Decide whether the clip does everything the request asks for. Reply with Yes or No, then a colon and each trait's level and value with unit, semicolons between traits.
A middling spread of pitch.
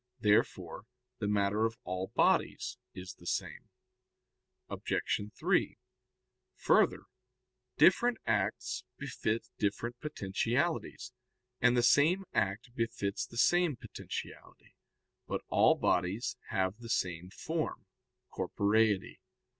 Yes: average, 4.0 semitones